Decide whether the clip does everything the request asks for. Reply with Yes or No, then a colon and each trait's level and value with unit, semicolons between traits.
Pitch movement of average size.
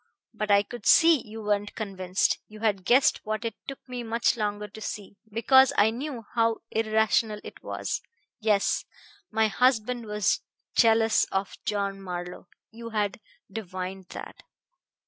No: narrow, 2.1 semitones